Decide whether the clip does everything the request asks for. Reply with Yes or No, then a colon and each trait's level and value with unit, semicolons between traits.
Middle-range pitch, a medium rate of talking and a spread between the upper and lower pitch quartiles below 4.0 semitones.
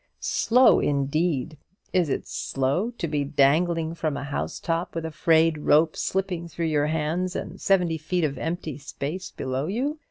Yes: medium, 160 Hz; average, 160 wpm; average, 3.2 semitones